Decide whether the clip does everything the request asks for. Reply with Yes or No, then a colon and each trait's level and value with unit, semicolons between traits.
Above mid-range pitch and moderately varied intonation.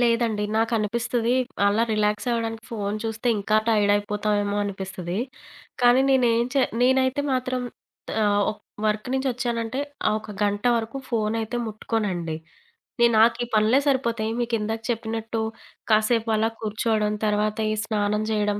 No: high, 220 Hz; narrow, 2.0 semitones